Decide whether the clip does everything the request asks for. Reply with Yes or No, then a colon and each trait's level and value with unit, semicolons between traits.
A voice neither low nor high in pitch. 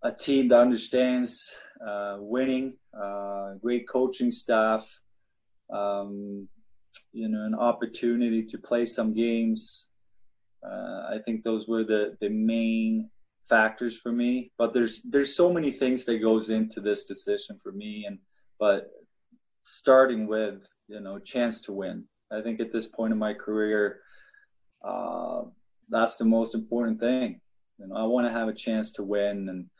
No: low, 115 Hz